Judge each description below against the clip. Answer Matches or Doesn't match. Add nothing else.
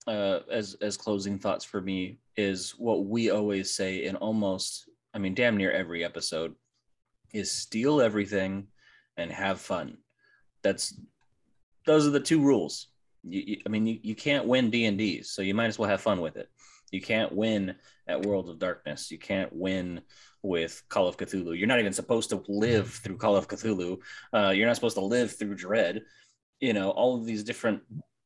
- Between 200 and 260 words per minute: Doesn't match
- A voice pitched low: Matches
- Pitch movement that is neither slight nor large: Matches